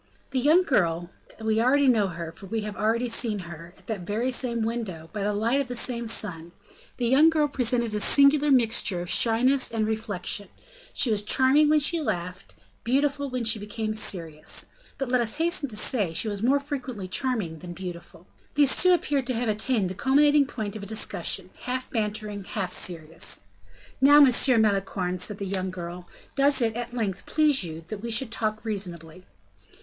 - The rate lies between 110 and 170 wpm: No, average, 185 wpm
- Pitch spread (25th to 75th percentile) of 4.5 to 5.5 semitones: Yes, average, 5.1 semitones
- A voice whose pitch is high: Yes, high, 220 Hz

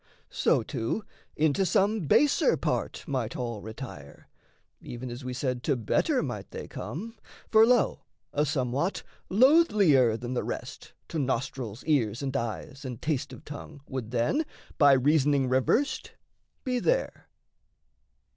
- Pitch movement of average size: No, wide, 6.1 semitones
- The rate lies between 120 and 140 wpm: Yes, slow, 135 wpm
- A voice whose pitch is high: No, low, 135 Hz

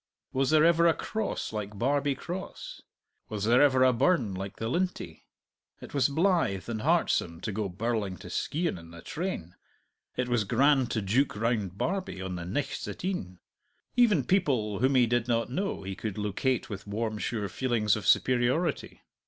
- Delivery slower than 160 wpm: No, average, 175 wpm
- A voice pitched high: No, low, 120 Hz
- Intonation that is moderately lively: No, wide, 6.0 semitones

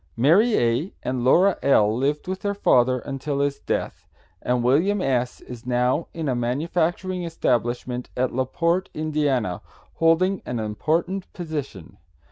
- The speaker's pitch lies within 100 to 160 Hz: Yes, medium, 140 Hz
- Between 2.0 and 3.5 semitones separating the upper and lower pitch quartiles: No, wide, 5.5 semitones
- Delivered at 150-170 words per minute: No, average, 140 wpm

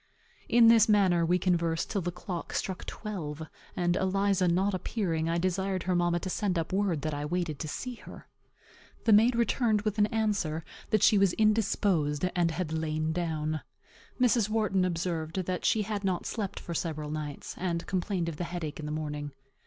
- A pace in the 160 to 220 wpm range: Yes, average, 185 wpm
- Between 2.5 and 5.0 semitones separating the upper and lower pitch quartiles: Yes, average, 3.9 semitones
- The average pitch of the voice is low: No, medium, 180 Hz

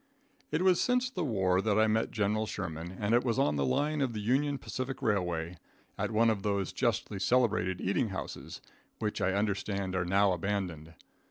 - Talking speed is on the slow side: No, average, 185 wpm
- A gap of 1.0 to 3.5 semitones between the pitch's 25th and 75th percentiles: No, average, 4.3 semitones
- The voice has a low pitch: Yes, low, 105 Hz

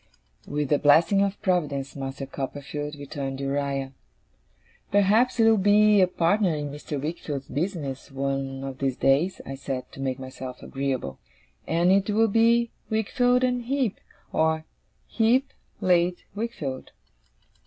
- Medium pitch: Yes, medium, 155 Hz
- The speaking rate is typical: No, slow, 130 wpm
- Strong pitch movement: Yes, wide, 7.0 semitones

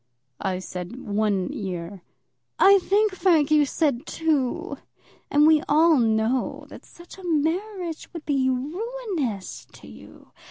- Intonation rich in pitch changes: Yes, wide, 7.8 semitones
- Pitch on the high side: Yes, very high, 290 Hz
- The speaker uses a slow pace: Yes, slow, 130 wpm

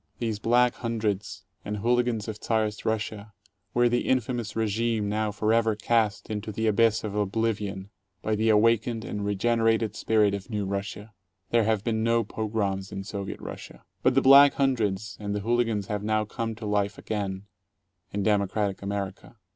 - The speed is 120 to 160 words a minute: No, average, 170 wpm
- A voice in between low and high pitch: No, low, 110 Hz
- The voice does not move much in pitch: Yes, narrow, 1.9 semitones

